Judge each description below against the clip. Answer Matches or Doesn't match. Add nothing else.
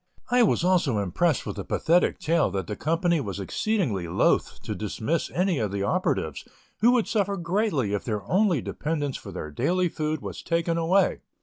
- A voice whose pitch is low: Doesn't match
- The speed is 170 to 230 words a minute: Matches